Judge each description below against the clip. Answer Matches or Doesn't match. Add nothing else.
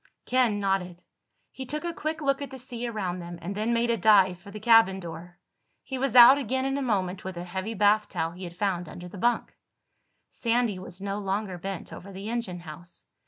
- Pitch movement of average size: Matches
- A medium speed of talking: Doesn't match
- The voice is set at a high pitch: Matches